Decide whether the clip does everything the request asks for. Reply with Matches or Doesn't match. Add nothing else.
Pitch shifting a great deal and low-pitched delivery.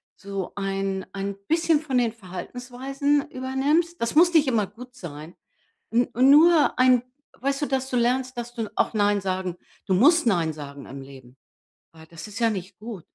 Doesn't match